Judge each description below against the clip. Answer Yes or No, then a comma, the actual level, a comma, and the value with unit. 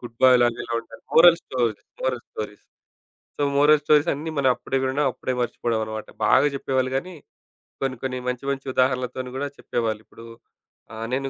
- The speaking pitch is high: No, low, 130 Hz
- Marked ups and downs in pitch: No, narrow, 2.6 semitones